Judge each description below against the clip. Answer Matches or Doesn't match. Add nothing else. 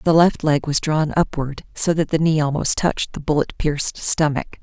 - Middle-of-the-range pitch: Matches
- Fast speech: Matches